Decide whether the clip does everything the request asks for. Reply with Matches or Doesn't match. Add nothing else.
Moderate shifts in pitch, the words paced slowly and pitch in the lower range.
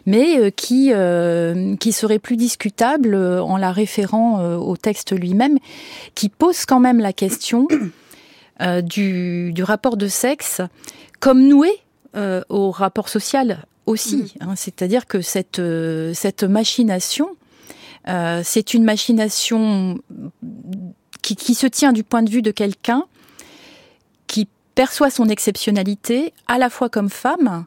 Doesn't match